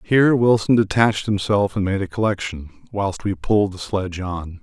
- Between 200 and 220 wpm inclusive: No, average, 180 wpm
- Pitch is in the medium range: No, low, 100 Hz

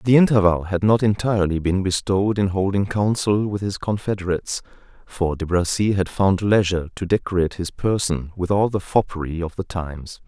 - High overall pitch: No, very low, 95 Hz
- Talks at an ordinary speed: Yes, average, 175 wpm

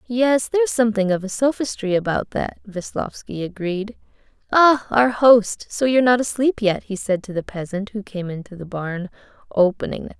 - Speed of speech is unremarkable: Yes, average, 190 wpm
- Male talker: No, female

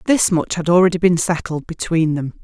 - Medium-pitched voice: Yes, medium, 170 Hz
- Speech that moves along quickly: No, average, 195 wpm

